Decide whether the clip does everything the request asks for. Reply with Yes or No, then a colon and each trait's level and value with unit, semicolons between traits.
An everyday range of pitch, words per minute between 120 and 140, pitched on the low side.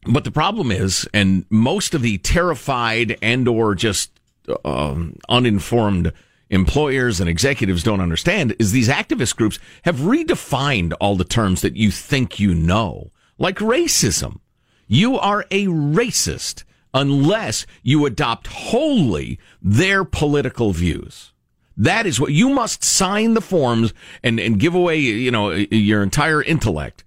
No: wide, 7.2 semitones; slow, 135 wpm; low, 115 Hz